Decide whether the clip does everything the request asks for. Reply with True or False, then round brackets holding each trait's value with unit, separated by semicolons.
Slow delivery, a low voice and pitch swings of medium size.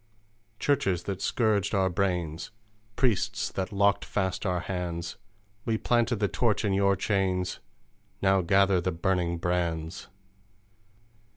False (120 wpm; 95 Hz; 2.2 semitones)